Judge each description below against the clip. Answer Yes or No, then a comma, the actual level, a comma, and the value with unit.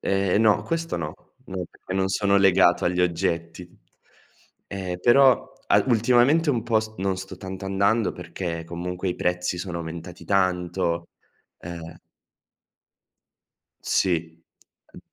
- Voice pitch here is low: Yes, very low, 95 Hz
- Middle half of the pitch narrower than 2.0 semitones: No, narrow, 2.4 semitones